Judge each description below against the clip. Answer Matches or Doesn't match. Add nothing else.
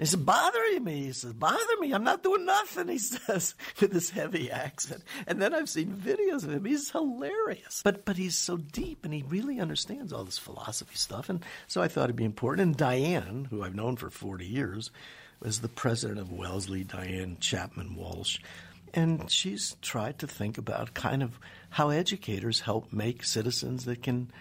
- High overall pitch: Doesn't match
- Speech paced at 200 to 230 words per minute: Doesn't match